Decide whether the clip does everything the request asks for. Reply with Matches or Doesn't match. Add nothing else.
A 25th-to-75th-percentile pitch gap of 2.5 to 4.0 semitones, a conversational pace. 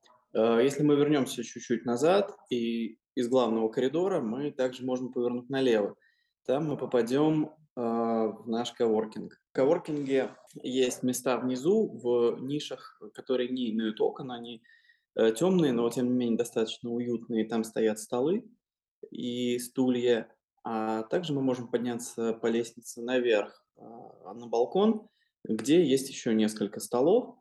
Matches